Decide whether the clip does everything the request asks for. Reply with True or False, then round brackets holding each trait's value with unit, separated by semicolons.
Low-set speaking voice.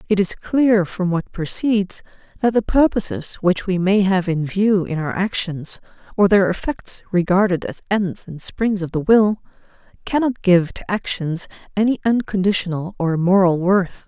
False (190 Hz)